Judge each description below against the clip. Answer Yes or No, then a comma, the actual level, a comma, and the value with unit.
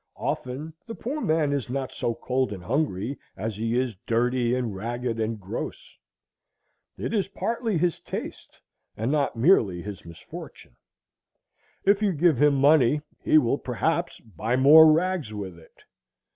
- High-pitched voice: No, low, 125 Hz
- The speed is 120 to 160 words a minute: Yes, average, 150 wpm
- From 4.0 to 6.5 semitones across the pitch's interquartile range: Yes, wide, 5.6 semitones